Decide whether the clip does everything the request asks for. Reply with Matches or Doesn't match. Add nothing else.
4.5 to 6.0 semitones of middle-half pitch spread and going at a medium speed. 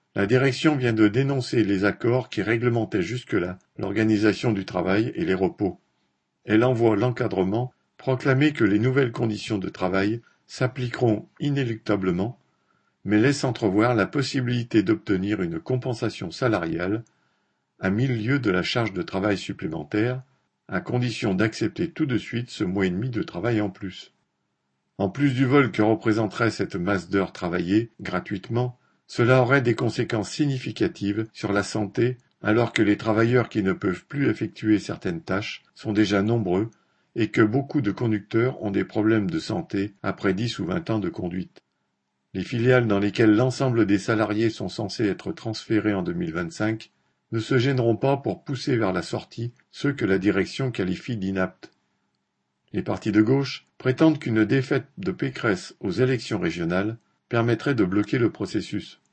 Doesn't match